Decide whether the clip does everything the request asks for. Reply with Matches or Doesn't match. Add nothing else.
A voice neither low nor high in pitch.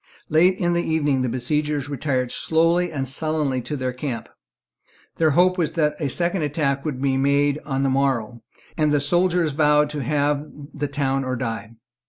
Matches